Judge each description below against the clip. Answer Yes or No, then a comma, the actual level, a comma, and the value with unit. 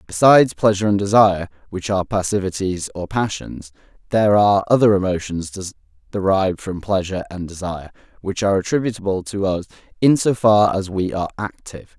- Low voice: Yes, very low, 95 Hz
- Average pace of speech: Yes, average, 150 wpm